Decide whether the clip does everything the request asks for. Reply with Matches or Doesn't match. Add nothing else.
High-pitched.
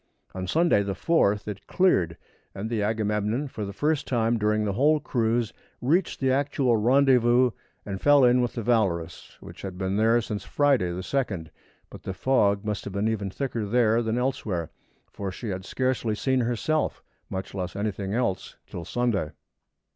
Doesn't match